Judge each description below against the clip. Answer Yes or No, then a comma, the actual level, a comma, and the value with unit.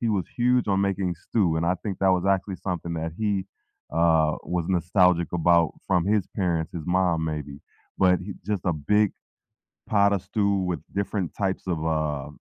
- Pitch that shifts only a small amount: No, average, 3.0 semitones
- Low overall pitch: Yes, very low, 90 Hz